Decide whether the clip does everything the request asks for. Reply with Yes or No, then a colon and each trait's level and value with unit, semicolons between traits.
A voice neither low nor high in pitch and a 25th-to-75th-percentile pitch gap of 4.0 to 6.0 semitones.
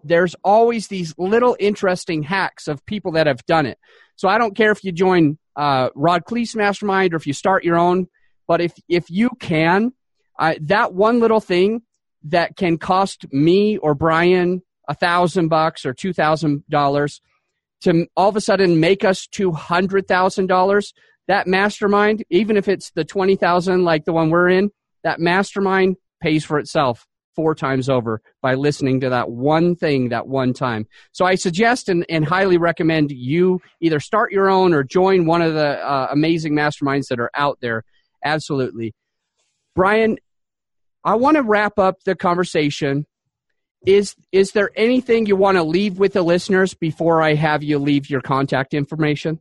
Yes: medium, 175 Hz; average, 4.3 semitones